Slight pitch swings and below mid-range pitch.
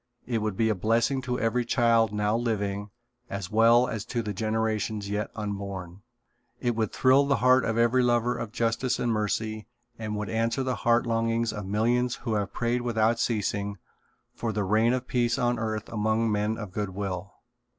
Yes: narrow, 2.2 semitones; low, 110 Hz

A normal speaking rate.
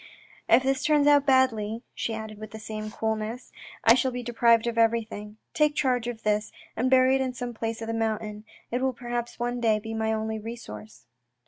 No: fast, 215 wpm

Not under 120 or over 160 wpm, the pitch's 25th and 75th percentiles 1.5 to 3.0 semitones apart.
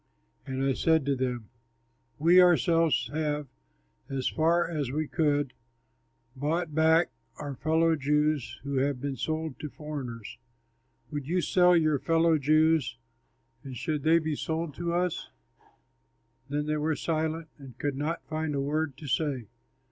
Yes: average, 150 wpm; narrow, 2.5 semitones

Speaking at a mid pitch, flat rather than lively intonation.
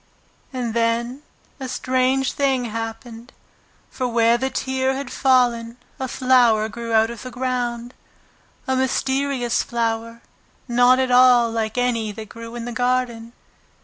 No: high, 245 Hz; narrow, 1.9 semitones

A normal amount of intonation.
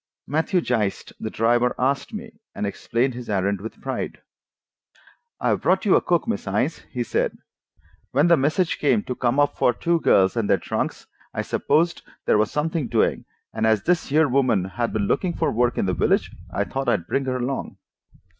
No: wide, 6.1 semitones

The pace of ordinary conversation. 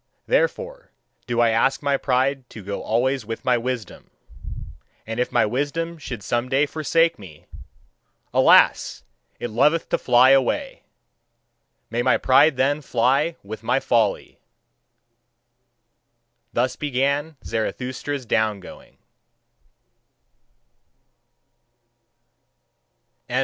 No: slow, 100 wpm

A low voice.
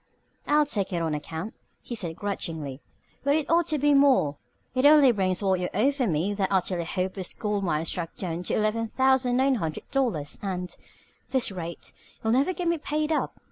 No: high, 205 Hz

